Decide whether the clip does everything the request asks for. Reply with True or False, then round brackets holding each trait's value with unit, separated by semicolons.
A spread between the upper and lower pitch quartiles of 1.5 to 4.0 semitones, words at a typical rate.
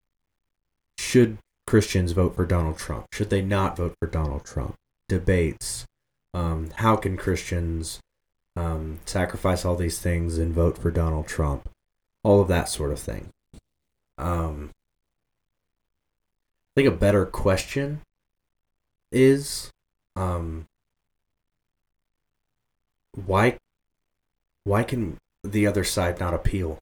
False (3.7 semitones; 110 wpm)